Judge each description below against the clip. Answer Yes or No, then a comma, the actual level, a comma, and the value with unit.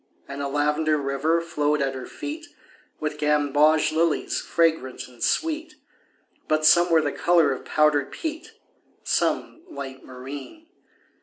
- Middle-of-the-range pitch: Yes, medium, 150 Hz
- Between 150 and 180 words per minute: No, slow, 135 wpm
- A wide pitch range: No, average, 3.1 semitones